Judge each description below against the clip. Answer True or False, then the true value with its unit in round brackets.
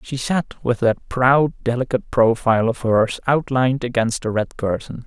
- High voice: False (125 Hz)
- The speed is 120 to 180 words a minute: True (165 wpm)